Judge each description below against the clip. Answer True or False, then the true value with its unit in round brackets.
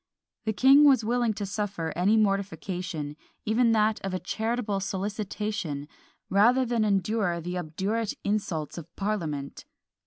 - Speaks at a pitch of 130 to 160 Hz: False (205 Hz)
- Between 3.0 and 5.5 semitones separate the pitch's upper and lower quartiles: True (3.5 semitones)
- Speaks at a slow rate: True (130 wpm)